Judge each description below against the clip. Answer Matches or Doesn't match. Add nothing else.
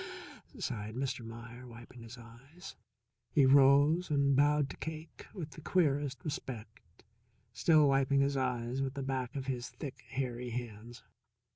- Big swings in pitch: Doesn't match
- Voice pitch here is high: Doesn't match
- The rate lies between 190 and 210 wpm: Doesn't match